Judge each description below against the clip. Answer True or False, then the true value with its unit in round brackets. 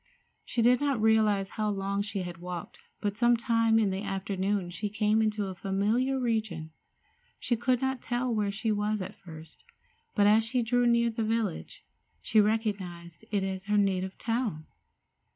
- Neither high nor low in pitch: False (210 Hz)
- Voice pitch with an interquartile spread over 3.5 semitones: False (2.9 semitones)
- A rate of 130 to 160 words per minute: False (175 wpm)